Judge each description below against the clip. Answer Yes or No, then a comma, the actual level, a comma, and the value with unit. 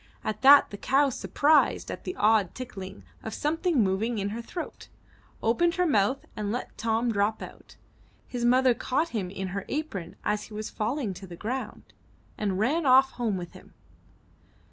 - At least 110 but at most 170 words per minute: No, average, 180 wpm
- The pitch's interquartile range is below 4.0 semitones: No, average, 4.8 semitones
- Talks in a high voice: Yes, high, 225 Hz